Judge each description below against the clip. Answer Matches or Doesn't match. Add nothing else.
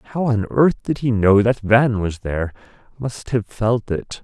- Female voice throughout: Doesn't match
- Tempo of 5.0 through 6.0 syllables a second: Doesn't match